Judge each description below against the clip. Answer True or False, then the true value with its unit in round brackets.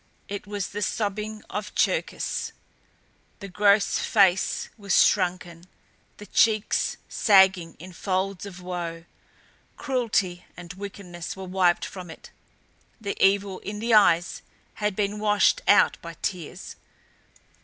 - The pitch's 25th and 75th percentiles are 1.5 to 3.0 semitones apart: True (2.6 semitones)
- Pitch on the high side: True (195 Hz)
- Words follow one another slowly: True (120 wpm)